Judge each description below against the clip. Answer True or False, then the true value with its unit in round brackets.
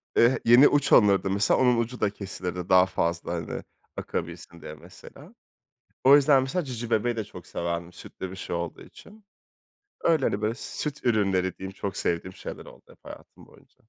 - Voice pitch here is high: False (100 Hz)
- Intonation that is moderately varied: False (5.8 semitones)